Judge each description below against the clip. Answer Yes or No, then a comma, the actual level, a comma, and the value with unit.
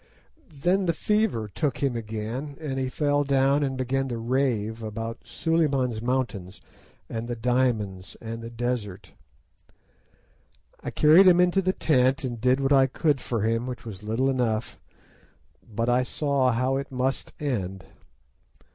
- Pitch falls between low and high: No, low, 130 Hz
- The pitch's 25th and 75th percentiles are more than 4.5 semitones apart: No, average, 3.4 semitones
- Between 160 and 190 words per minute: No, average, 150 wpm